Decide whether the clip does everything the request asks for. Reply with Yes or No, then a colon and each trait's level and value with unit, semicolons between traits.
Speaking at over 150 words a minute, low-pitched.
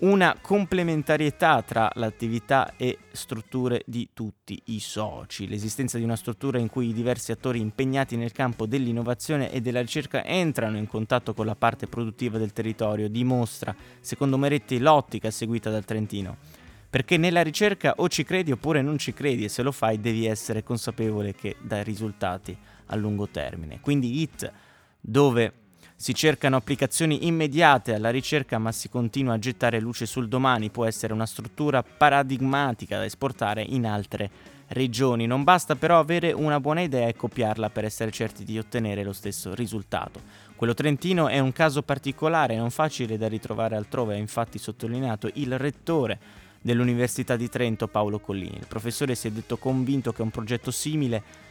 Yes: average, 165 wpm; low, 120 Hz